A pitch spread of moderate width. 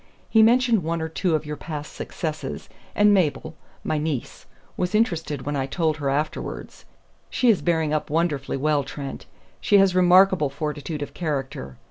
Yes: average, 3.7 semitones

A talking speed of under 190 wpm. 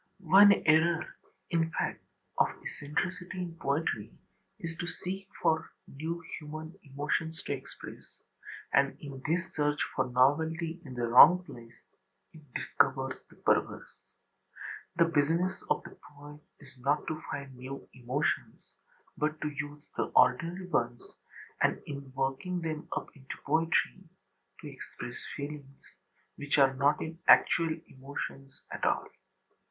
Yes: slow, 135 wpm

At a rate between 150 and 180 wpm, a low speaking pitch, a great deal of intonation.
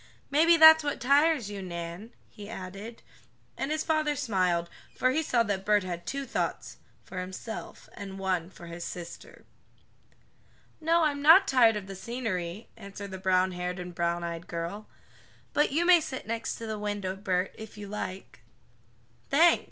No: average, 160 wpm; high, 205 Hz; wide, 7.0 semitones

